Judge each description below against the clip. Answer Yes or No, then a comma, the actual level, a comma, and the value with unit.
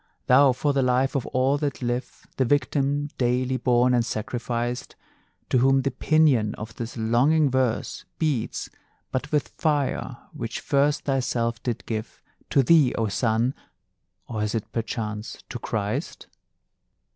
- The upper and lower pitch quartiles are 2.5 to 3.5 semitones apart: Yes, average, 2.9 semitones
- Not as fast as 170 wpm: Yes, average, 145 wpm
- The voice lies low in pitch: Yes, low, 125 Hz